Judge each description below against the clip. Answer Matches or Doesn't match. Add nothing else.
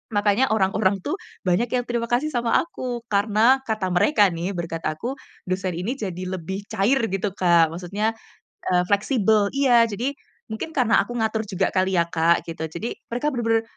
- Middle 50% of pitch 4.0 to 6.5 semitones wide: Matches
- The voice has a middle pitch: Doesn't match